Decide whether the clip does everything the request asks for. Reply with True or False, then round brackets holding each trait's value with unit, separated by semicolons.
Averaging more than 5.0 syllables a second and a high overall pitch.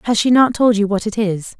True (5.7 syllables/s; 215 Hz)